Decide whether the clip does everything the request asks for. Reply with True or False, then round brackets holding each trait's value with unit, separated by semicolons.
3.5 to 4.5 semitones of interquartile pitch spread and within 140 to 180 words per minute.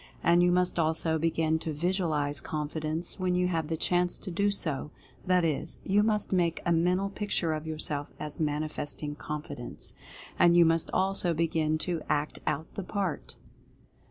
False (2.7 semitones; 170 wpm)